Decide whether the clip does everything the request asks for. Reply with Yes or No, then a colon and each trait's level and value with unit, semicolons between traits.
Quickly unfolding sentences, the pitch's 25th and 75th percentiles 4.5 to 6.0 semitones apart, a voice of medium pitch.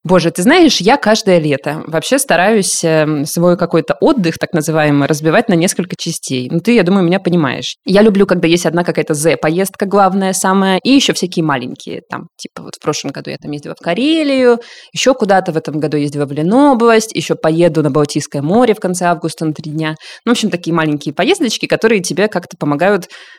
Yes: fast, 200 wpm; average, 4.9 semitones; medium, 175 Hz